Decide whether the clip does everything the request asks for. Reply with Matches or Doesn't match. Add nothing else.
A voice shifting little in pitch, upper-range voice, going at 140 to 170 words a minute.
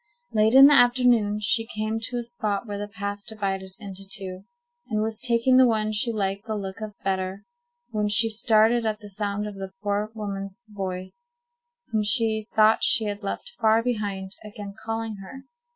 Doesn't match